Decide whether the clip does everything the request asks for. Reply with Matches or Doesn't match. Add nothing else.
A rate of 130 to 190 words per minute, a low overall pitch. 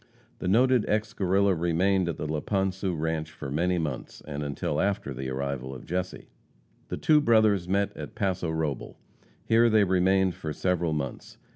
Matches